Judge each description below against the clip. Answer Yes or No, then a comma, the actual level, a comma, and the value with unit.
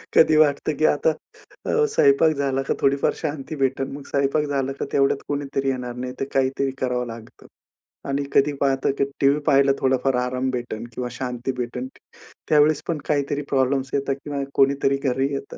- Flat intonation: Yes, narrow, 1.5 semitones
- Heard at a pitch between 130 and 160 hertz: Yes, low, 135 Hz